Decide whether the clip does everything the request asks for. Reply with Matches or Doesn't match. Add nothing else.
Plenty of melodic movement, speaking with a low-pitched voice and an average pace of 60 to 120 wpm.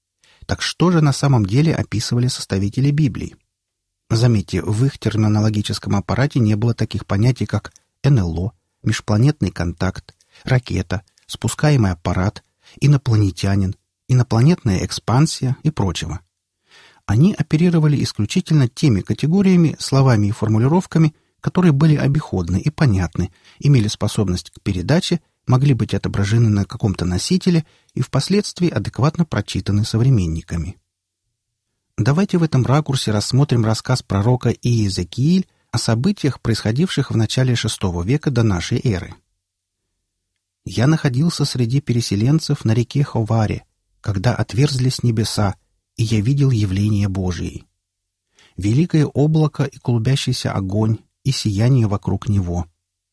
Matches